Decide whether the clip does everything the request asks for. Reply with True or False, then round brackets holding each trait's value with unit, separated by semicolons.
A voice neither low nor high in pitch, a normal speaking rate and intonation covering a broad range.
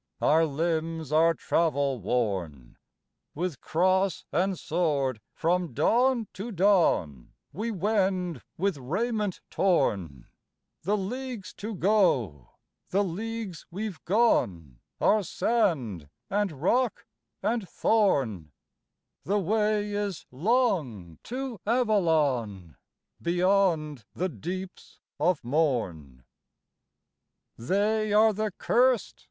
False (180 Hz; 100 wpm; 7.5 semitones)